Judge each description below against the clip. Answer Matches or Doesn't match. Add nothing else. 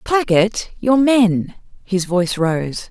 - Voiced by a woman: Matches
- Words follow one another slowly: Matches